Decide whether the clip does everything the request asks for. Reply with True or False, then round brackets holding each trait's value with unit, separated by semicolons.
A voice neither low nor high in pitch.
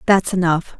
True (180 Hz)